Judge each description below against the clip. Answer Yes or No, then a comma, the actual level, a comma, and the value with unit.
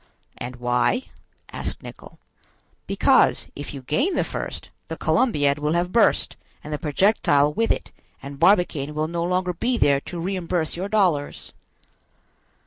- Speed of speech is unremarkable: Yes, average, 145 wpm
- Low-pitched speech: No, medium, 170 Hz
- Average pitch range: Yes, average, 4.9 semitones